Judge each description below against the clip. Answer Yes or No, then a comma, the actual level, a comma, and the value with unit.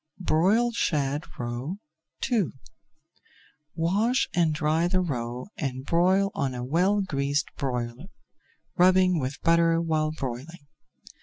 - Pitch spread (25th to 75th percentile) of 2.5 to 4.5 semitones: No, average, 5.0 semitones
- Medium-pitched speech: Yes, medium, 160 Hz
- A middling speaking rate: No, slow, 110 wpm